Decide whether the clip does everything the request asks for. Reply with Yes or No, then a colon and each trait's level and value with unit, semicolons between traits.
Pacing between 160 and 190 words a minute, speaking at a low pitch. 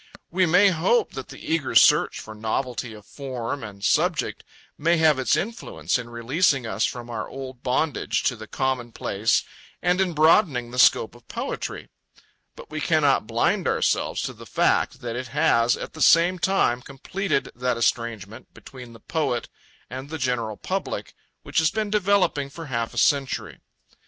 Yes: average, 165 wpm; low, 130 Hz